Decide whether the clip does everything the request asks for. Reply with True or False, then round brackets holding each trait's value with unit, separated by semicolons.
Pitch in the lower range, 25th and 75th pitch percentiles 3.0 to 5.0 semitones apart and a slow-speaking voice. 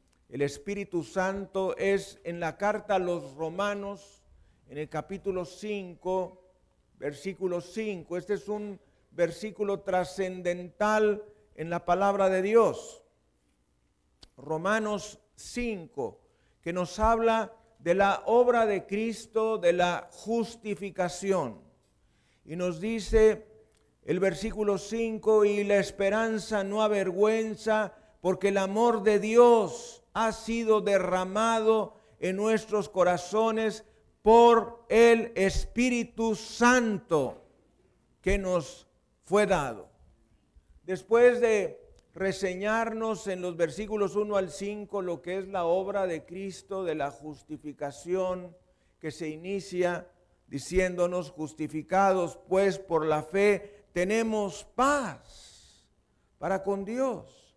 False (195 Hz; 3.6 semitones; 105 wpm)